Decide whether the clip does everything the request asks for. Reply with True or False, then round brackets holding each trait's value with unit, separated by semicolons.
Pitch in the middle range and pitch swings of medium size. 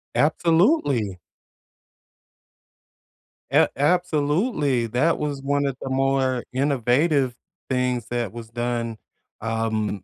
False (130 Hz; 3.6 semitones)